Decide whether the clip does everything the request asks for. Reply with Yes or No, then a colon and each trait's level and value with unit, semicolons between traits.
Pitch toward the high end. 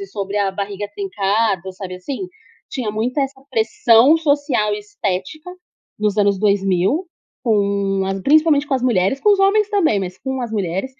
Yes: high, 210 Hz